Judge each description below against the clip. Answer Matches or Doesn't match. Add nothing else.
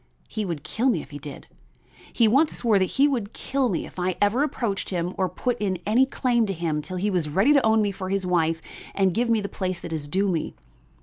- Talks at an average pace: Doesn't match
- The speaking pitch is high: Matches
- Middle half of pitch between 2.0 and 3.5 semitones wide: Doesn't match